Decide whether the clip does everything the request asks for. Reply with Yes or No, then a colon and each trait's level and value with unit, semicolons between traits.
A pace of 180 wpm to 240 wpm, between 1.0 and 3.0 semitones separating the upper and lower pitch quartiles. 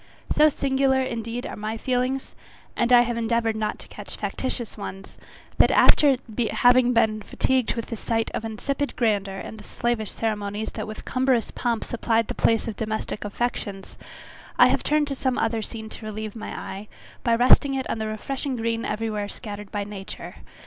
Yes: average, 185 wpm; narrow, 2.6 semitones